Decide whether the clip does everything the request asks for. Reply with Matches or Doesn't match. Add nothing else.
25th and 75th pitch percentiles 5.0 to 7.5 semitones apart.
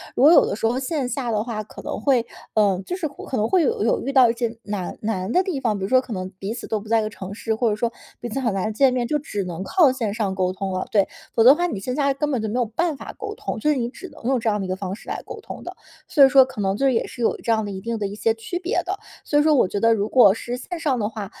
Doesn't match